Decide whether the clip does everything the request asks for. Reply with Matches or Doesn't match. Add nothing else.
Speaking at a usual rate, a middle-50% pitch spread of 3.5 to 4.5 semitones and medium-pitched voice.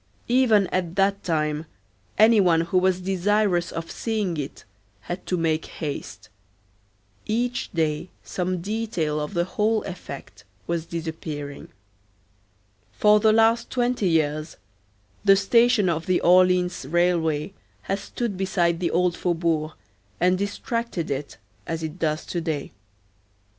Doesn't match